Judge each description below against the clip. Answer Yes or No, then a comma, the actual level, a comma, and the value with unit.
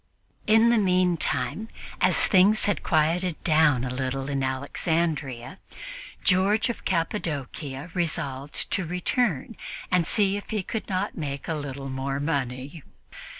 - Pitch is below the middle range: No, medium, 160 Hz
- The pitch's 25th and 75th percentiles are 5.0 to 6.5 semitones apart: Yes, wide, 5.5 semitones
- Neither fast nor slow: No, slow, 130 wpm